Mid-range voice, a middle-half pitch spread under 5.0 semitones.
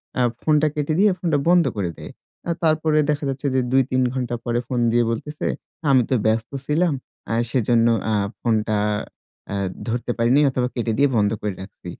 No: low, 130 Hz; average, 4.5 semitones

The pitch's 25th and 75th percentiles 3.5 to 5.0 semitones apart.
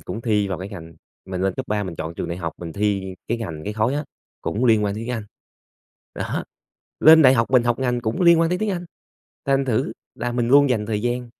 Yes: average, 4.3 semitones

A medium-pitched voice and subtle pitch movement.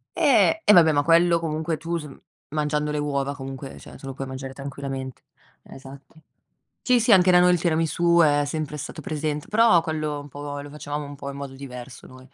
No: medium, 150 Hz; average, 3.0 semitones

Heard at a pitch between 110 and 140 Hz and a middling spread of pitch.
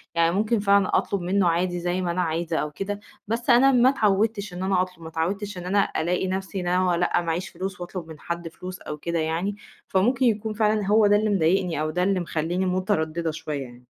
No: medium, 185 Hz; average, 3.2 semitones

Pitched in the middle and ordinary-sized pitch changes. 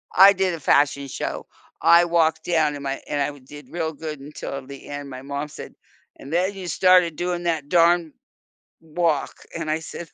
Yes: medium, 160 Hz; average, 3.2 semitones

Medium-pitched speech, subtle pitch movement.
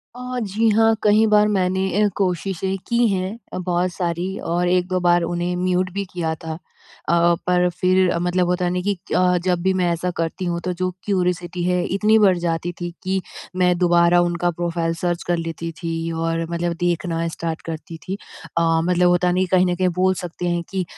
Yes: medium, 180 Hz; narrow, 1.4 semitones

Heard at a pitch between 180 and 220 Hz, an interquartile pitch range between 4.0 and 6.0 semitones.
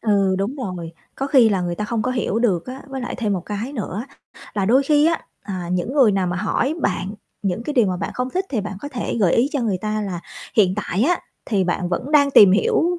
Yes: high, 215 Hz; wide, 5.6 semitones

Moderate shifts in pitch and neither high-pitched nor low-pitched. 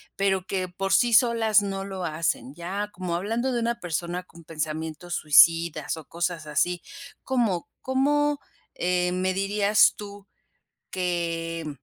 Yes: average, 3.6 semitones; medium, 180 Hz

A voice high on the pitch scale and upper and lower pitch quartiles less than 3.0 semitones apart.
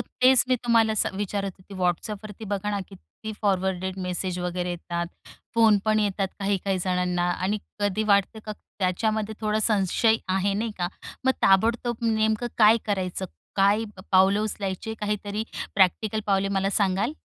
Yes: high, 200 Hz; narrow, 2.4 semitones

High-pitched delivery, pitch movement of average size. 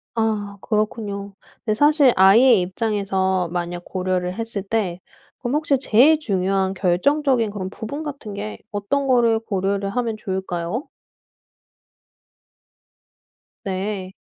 Yes: high, 205 Hz; average, 3.8 semitones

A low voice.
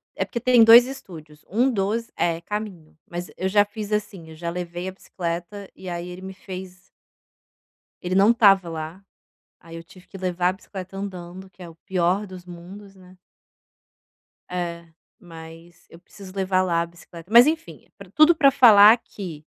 No: medium, 185 Hz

